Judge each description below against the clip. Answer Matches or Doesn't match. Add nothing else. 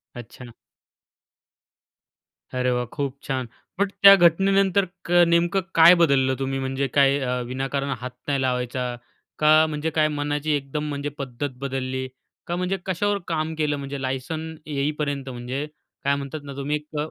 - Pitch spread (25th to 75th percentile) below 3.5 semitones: Matches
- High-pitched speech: Doesn't match